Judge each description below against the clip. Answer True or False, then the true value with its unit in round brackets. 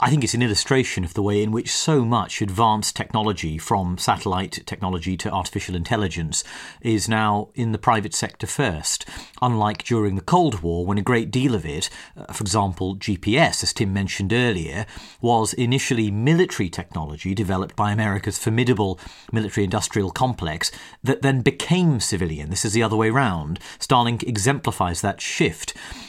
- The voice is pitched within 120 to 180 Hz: False (105 Hz)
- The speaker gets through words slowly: False (160 wpm)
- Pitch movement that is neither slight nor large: True (3.9 semitones)